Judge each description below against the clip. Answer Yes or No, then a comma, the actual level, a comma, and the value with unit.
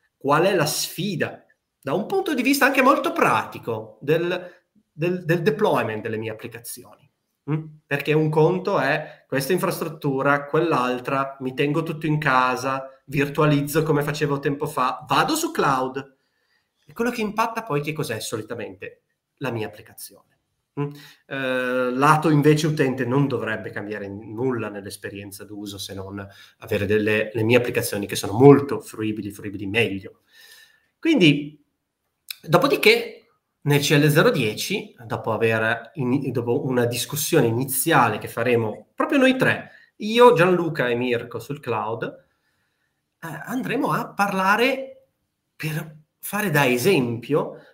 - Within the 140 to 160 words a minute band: No, average, 130 wpm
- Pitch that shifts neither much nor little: No, wide, 5.8 semitones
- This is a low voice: No, medium, 145 Hz